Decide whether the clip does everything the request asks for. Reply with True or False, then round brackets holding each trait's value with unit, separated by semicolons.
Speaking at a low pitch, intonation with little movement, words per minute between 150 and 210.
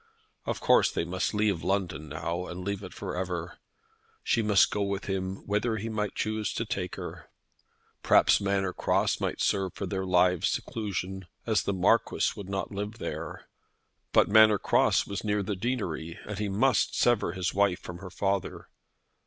True (100 Hz; 2.3 semitones; 175 wpm)